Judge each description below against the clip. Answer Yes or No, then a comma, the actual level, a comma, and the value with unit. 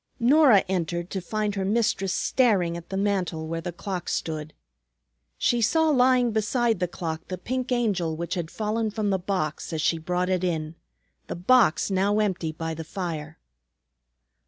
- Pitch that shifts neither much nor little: Yes, average, 4.5 semitones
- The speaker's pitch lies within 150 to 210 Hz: Yes, high, 190 Hz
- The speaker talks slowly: No, average, 170 wpm